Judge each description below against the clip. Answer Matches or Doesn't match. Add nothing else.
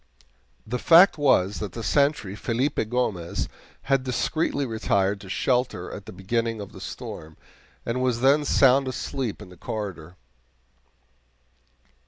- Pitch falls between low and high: Doesn't match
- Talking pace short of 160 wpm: Matches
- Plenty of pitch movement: Doesn't match